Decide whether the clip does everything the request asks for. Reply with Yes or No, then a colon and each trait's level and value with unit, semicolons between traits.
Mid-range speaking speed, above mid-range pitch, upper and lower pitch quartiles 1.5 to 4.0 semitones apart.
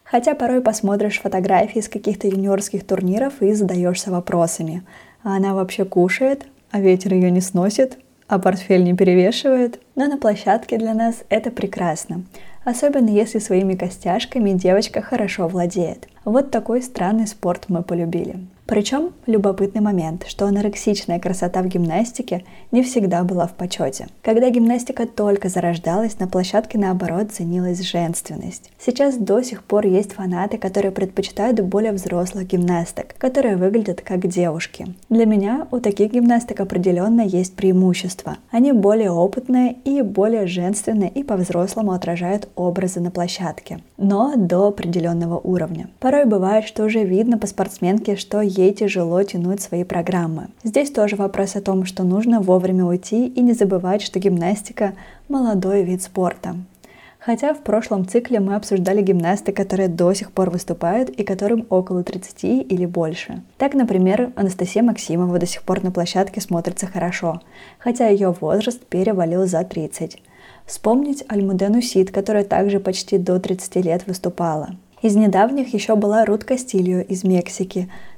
Yes: average, 145 wpm; high, 195 Hz; average, 3.2 semitones